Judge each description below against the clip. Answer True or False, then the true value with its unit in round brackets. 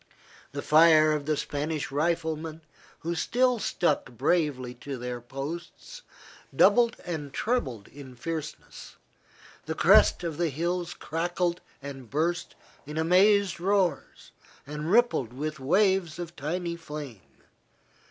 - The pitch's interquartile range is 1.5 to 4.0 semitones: True (3.6 semitones)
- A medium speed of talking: False (120 wpm)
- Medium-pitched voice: True (160 Hz)